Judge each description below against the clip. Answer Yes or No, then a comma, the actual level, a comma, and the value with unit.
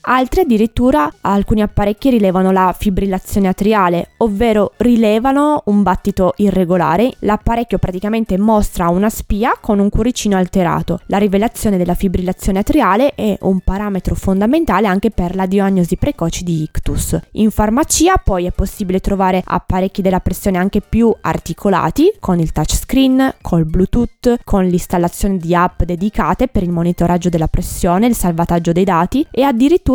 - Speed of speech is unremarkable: Yes, average, 140 wpm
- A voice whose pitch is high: Yes, high, 200 Hz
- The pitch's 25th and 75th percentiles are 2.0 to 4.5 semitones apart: Yes, average, 3.8 semitones